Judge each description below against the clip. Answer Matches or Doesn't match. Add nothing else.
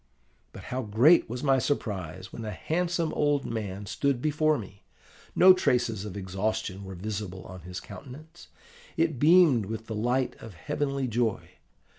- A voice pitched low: Matches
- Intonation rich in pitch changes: Matches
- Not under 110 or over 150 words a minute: Doesn't match